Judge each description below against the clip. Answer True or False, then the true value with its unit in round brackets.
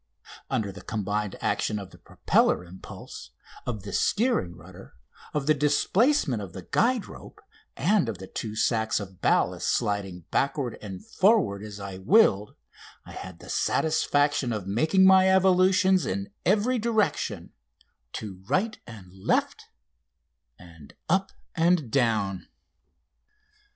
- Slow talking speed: True (130 wpm)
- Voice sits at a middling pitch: False (110 Hz)